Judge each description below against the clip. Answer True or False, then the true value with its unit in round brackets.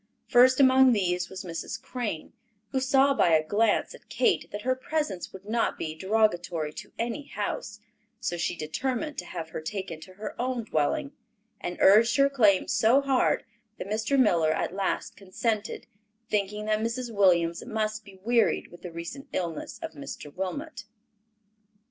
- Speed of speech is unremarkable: True (165 wpm)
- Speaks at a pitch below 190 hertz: False (210 Hz)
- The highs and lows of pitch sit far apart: True (6.1 semitones)